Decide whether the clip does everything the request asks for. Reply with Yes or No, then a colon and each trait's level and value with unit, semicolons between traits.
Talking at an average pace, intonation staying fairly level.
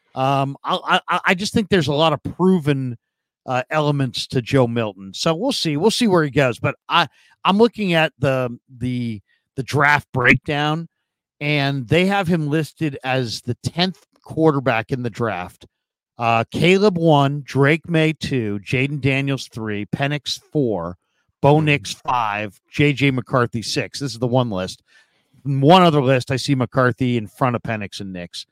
No: average, 170 wpm; average, 4.2 semitones